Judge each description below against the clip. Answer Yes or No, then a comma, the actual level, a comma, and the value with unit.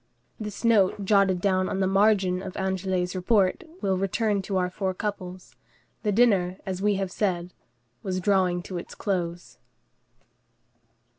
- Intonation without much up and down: Yes, narrow, 1.7 semitones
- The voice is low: No, high, 190 Hz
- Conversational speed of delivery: Yes, average, 150 wpm